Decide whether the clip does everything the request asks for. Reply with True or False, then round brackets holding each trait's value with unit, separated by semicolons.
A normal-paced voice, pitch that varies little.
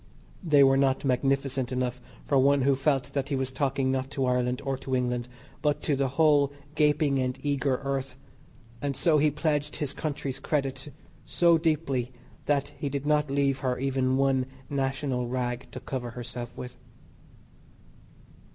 True (160 wpm; 1.8 semitones)